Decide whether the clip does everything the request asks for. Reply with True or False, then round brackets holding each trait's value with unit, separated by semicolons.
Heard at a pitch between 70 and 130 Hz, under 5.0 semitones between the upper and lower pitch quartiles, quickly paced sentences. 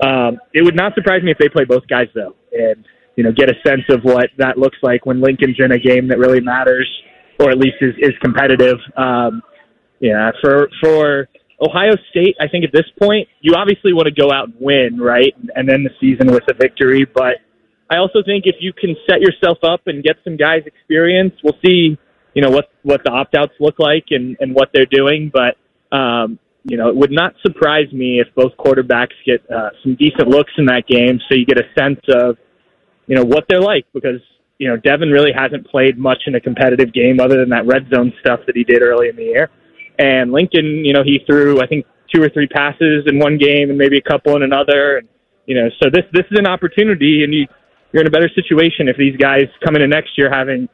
False (140 Hz; 3.9 semitones; 230 wpm)